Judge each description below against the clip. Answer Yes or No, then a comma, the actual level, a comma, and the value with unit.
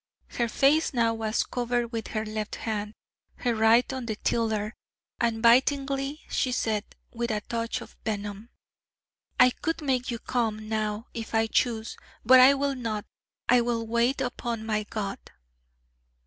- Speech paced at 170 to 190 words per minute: No, average, 155 wpm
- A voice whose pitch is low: No, high, 230 Hz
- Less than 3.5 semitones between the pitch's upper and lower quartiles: Yes, narrow, 2.4 semitones